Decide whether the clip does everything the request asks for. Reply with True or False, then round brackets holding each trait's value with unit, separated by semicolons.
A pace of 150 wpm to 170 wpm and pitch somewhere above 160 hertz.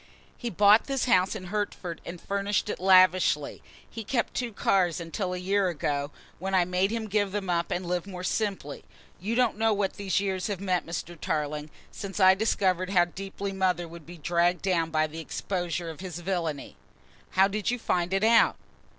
False (195 wpm; 185 Hz)